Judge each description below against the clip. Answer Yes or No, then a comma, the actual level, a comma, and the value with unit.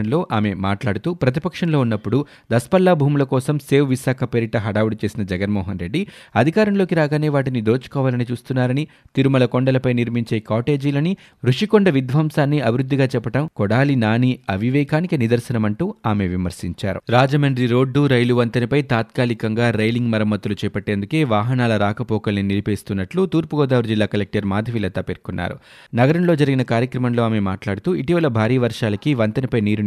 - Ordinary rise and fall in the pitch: Yes, average, 4.9 semitones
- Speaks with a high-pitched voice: No, low, 125 Hz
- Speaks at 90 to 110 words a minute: No, average, 120 wpm